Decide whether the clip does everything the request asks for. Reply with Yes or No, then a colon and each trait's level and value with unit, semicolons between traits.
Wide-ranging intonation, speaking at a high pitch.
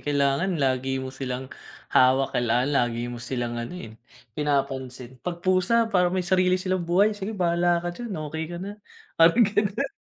No: wide, 6.1 semitones; medium, 165 Hz